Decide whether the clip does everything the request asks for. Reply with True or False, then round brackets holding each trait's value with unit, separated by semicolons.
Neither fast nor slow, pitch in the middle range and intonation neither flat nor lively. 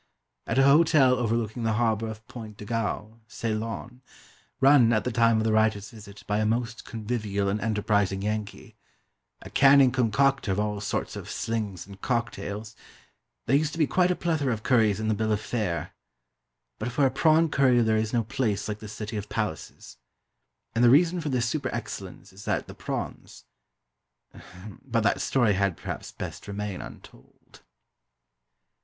False (175 wpm; 110 Hz; 3.3 semitones)